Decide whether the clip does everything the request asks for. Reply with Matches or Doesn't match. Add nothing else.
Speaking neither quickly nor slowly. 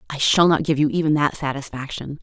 Doesn't match